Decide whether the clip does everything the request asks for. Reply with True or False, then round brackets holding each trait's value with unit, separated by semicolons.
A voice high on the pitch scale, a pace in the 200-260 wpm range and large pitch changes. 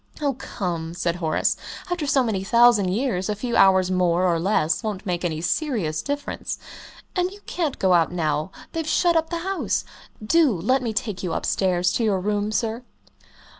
False (205 Hz; 180 wpm; 6.9 semitones)